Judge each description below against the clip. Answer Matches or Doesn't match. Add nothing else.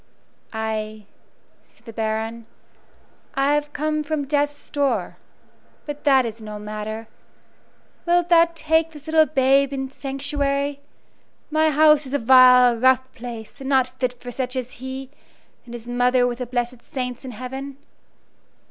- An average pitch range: Matches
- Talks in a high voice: Matches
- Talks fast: Doesn't match